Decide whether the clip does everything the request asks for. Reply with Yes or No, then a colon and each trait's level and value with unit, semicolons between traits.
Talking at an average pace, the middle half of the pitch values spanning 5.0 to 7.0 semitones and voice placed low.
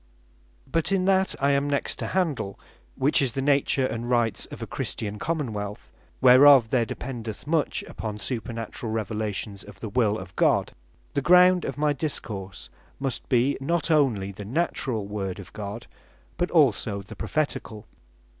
Yes: average, 160 wpm; wide, 5.5 semitones; low, 120 Hz